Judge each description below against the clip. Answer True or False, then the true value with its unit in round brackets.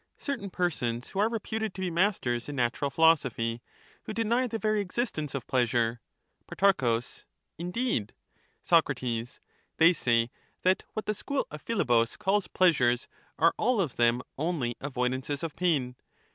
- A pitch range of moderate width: False (8.5 semitones)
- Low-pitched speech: False (155 Hz)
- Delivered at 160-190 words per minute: True (165 wpm)